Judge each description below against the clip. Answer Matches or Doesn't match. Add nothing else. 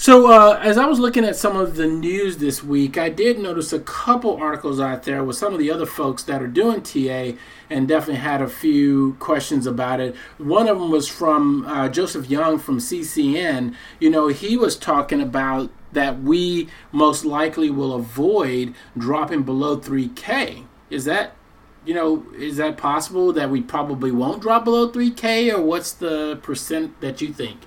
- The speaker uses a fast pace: Doesn't match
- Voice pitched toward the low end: Doesn't match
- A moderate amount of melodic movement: Doesn't match